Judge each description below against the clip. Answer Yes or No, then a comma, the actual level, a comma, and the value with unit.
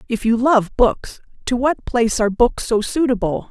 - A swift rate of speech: No, average, 190 wpm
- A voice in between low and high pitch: No, high, 235 Hz